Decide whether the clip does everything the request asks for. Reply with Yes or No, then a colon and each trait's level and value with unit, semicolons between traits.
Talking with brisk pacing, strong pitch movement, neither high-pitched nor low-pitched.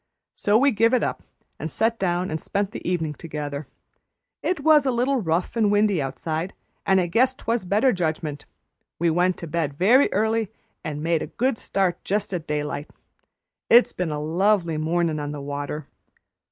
No: average, 180 wpm; wide, 5.9 semitones; medium, 180 Hz